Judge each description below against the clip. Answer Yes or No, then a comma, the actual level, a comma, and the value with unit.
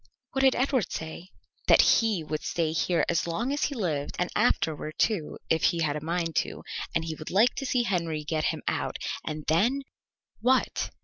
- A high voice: No, medium, 170 Hz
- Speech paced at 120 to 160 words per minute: No, average, 200 wpm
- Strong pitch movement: Yes, wide, 6.9 semitones